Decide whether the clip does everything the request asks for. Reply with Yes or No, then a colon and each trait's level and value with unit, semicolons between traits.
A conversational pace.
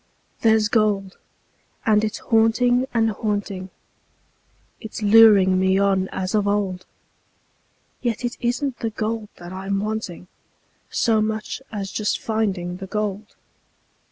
No: slow, 125 wpm